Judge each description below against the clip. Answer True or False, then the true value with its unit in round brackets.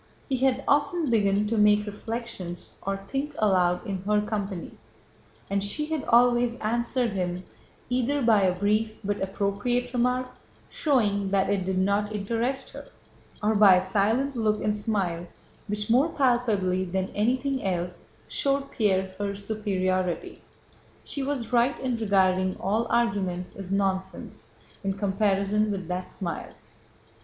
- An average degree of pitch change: True (3.9 semitones)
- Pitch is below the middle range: False (210 Hz)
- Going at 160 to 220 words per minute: False (135 wpm)